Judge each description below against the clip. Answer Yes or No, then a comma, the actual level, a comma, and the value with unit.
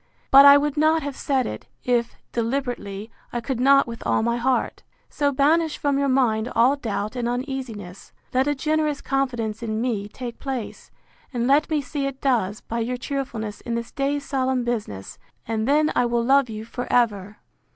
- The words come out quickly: No, average, 185 wpm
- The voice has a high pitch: Yes, very high, 250 Hz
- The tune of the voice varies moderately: Yes, average, 3.3 semitones